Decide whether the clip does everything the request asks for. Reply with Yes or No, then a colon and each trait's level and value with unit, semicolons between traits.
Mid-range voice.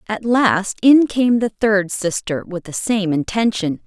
No: high, 205 Hz